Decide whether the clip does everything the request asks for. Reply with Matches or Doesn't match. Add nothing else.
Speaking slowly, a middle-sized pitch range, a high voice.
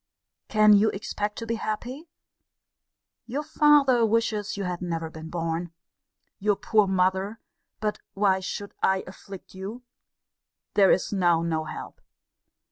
Matches